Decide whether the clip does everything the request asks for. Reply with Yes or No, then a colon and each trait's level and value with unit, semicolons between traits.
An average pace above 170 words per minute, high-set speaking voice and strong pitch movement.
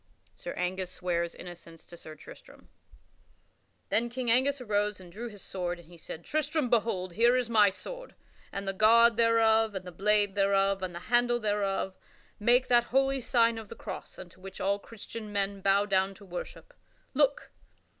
No: average, 180 wpm; high, 205 Hz; average, 3.9 semitones